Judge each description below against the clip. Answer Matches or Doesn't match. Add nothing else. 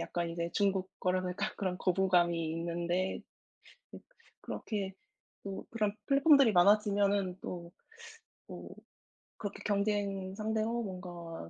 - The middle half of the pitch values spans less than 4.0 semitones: Matches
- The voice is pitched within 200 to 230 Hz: Doesn't match